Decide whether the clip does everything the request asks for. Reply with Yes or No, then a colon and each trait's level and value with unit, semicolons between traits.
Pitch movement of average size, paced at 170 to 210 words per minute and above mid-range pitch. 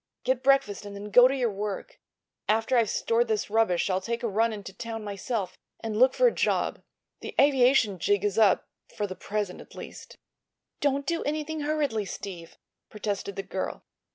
Yes: average, 4.3 semitones; average, 180 wpm; high, 220 Hz